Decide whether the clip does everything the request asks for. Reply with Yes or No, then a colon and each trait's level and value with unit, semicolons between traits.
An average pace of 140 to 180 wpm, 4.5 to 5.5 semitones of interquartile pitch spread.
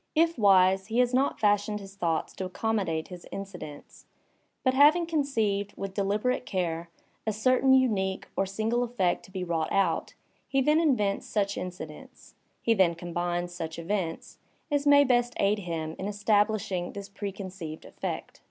Yes: average, 160 wpm; average, 5.0 semitones